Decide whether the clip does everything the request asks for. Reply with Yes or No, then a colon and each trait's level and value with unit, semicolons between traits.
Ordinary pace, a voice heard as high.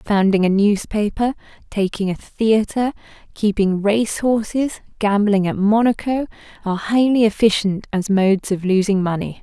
No: slow, 125 wpm; high, 210 Hz